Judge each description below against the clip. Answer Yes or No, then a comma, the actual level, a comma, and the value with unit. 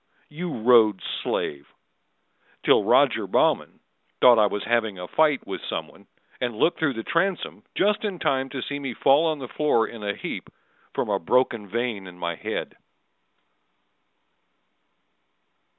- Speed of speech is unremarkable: Yes, average, 150 wpm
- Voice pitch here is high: No, low, 120 Hz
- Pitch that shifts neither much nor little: No, wide, 5.9 semitones